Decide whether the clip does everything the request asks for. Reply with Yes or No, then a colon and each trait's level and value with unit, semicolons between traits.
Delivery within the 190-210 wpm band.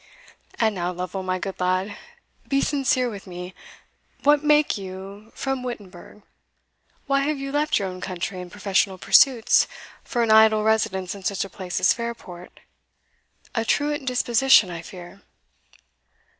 No: average, 145 wpm